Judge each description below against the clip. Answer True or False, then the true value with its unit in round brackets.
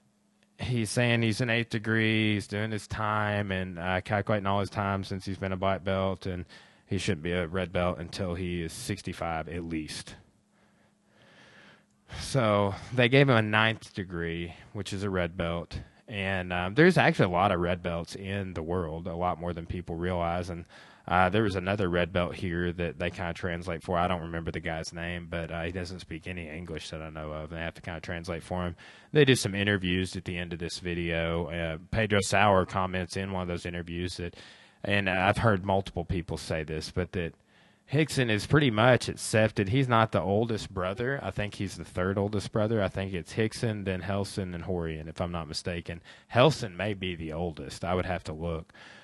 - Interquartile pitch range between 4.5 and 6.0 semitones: False (3.1 semitones)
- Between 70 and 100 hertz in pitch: True (95 Hz)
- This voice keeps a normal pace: False (210 wpm)